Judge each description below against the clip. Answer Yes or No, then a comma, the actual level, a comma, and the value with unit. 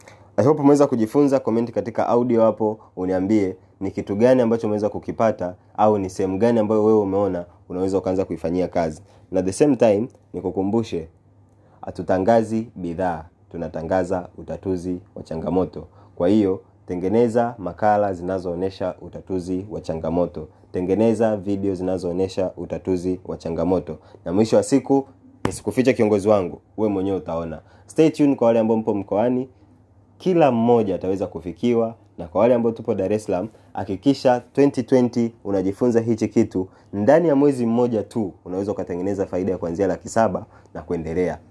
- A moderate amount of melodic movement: Yes, average, 3.7 semitones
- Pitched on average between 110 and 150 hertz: No, low, 100 Hz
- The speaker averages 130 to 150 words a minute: Yes, average, 135 wpm